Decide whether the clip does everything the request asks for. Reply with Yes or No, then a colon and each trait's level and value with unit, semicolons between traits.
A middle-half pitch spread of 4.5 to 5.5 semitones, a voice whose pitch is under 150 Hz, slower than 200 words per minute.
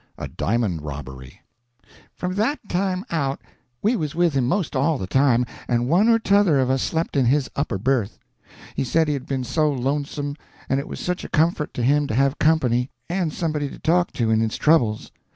No: average, 5.0 semitones; medium, 140 Hz; fast, 205 wpm